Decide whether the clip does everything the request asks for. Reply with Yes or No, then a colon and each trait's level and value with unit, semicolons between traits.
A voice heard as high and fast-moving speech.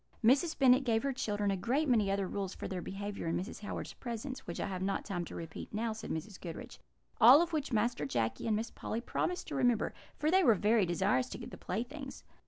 Yes: high, 220 Hz; fast, 230 wpm